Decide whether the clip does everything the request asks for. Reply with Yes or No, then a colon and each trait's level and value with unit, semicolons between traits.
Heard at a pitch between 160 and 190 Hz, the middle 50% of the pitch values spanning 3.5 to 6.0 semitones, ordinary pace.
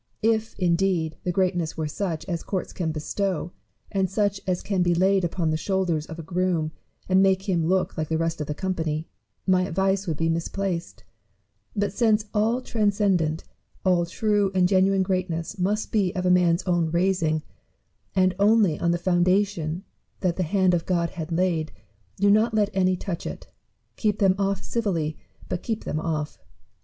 No: medium, 185 Hz; average, 2.8 semitones; average, 175 wpm